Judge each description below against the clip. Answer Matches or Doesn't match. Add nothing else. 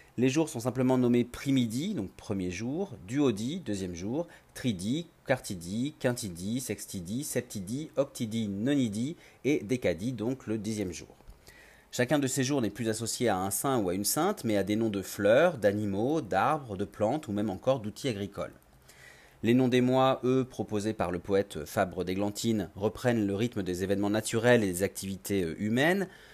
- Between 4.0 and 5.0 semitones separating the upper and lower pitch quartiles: Matches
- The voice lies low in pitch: Matches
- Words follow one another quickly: Doesn't match